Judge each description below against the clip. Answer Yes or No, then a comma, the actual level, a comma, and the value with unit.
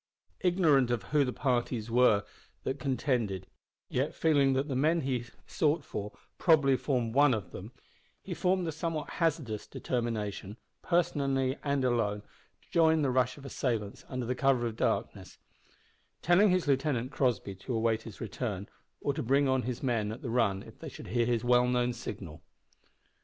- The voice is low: Yes, low, 125 Hz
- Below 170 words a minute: No, average, 180 wpm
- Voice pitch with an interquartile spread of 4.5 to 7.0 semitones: No, average, 3.8 semitones